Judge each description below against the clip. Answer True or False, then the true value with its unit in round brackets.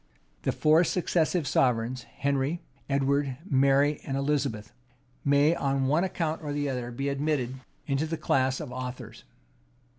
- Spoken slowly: True (130 wpm)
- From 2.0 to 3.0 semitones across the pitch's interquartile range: True (2.5 semitones)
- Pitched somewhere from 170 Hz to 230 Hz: False (140 Hz)